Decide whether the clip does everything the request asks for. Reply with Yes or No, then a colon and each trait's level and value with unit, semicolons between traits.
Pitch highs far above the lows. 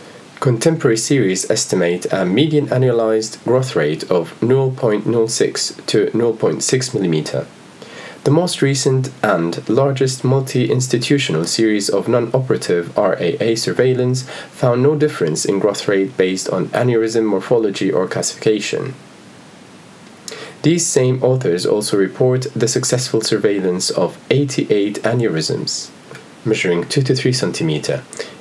No: average, 3.9 semitones